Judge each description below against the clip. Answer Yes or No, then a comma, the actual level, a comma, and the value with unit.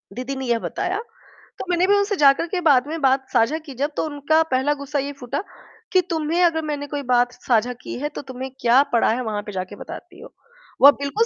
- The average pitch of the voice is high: Yes, very high, 280 Hz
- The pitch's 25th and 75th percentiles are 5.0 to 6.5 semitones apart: No, average, 4.2 semitones